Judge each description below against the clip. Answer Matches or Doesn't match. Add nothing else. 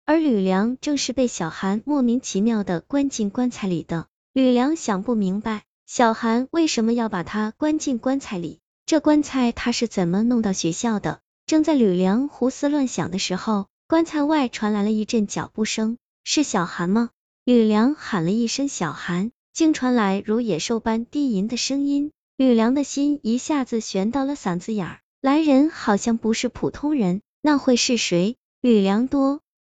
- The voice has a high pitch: Matches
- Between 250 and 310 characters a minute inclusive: Matches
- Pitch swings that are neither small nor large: Matches